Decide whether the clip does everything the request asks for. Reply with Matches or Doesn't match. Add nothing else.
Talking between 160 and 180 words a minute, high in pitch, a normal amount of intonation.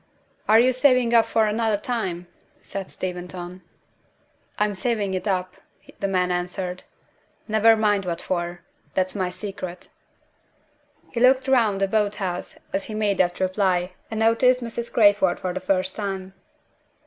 Doesn't match